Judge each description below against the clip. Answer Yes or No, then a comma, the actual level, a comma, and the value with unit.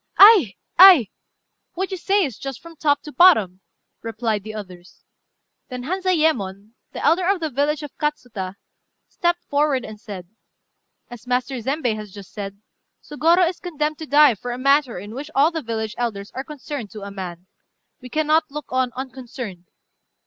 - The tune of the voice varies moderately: No, wide, 6.3 semitones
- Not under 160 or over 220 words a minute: Yes, average, 170 wpm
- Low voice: No, very high, 260 Hz